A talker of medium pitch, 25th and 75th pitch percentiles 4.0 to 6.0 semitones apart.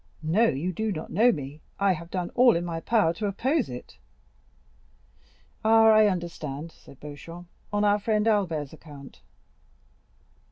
Yes: medium, 180 Hz; wide, 5.4 semitones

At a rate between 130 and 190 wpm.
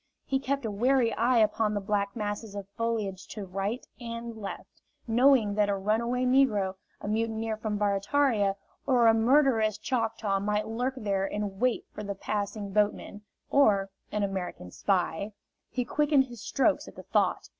Yes: average, 165 wpm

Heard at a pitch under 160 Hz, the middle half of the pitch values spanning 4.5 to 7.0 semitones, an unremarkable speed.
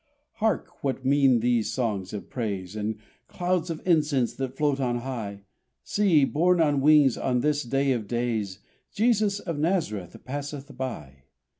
Yes: low, 135 Hz; average, 5.0 semitones; average, 150 wpm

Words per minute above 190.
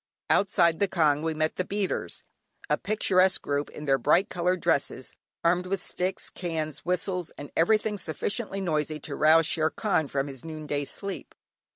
No: average, 165 wpm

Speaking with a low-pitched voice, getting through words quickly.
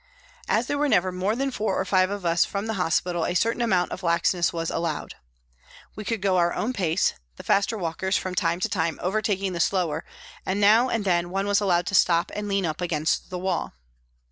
No: medium, 185 Hz; fast, 220 wpm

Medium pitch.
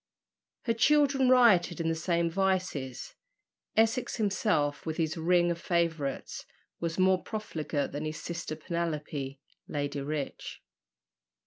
Yes: medium, 170 Hz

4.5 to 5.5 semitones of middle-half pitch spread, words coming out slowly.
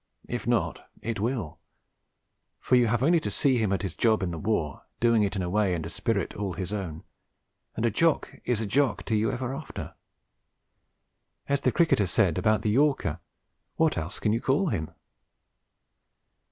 No: average, 5.0 semitones; average, 185 wpm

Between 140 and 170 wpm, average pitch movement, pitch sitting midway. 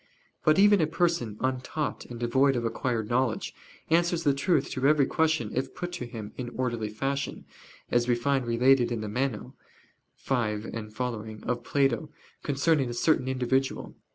No: average, 160 wpm; average, 3.2 semitones; low, 130 Hz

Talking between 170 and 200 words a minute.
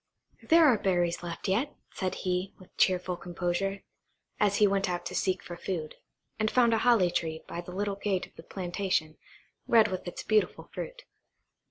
Yes: average, 180 wpm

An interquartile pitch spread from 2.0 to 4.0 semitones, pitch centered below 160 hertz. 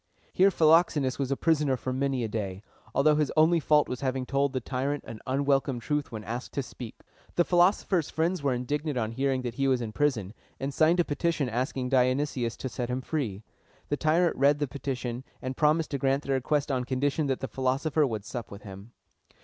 Yes: average, 2.9 semitones; low, 135 Hz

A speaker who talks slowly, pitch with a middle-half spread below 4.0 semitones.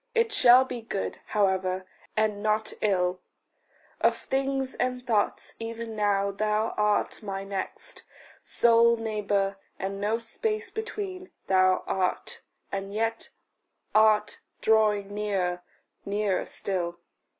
Yes: slow, 115 wpm; average, 2.8 semitones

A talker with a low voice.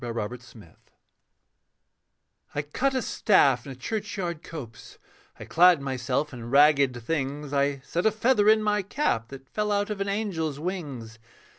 No: medium, 150 Hz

